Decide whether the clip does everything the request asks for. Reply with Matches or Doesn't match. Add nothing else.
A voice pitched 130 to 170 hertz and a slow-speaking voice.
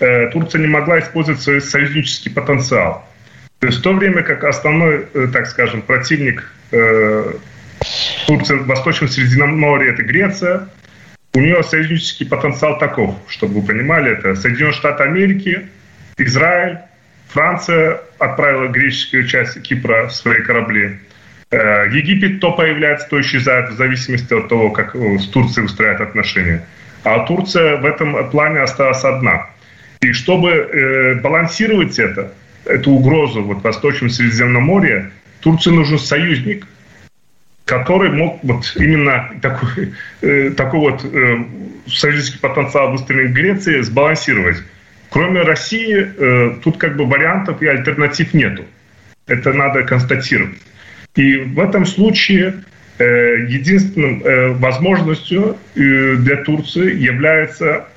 Doesn't match